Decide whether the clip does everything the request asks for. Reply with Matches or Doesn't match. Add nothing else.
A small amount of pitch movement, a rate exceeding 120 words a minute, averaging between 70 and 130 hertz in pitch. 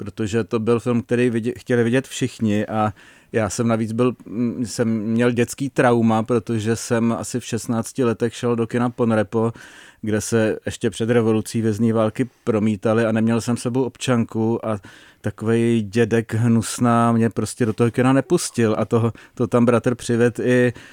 Matches